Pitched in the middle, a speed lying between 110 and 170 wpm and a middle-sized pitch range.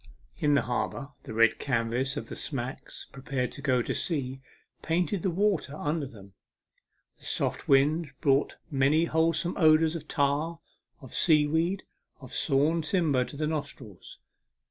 Yes: medium, 145 Hz; average, 145 wpm; average, 3.5 semitones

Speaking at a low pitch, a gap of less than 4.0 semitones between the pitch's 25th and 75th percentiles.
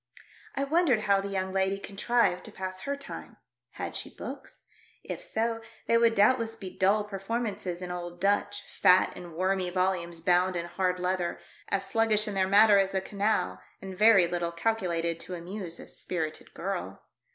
No: high, 190 Hz; average, 3.0 semitones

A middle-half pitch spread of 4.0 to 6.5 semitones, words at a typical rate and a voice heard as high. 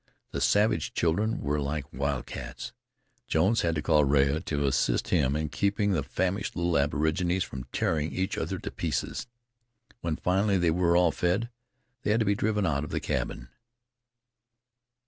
No: average, 4.9 semitones; average, 165 wpm; very low, 85 Hz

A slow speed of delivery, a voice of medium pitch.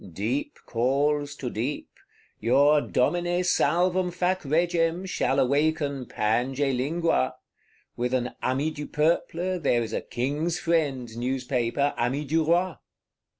Yes: slow, 120 wpm; medium, 145 Hz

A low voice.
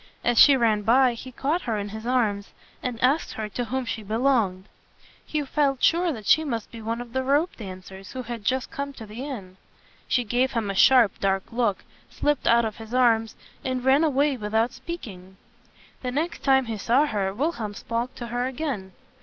No: high, 240 Hz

